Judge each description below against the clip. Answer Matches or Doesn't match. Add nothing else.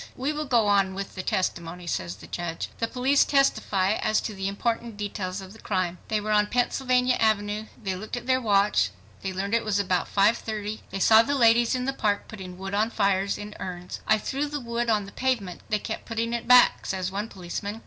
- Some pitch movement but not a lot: Matches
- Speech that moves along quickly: Matches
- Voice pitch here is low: Doesn't match